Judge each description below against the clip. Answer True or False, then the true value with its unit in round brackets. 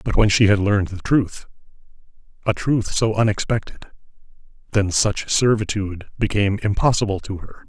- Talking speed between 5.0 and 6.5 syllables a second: True (5.5 syllables/s)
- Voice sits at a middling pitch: False (105 Hz)